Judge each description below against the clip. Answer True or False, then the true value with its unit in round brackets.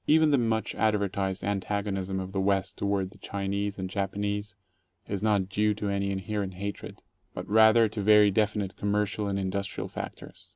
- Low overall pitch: True (100 Hz)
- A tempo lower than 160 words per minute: False (170 wpm)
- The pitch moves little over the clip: True (1.4 semitones)